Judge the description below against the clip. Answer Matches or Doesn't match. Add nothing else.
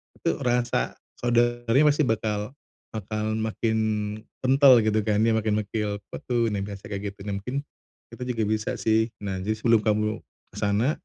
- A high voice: Doesn't match